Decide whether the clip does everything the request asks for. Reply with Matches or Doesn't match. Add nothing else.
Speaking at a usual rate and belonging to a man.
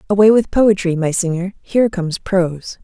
Doesn't match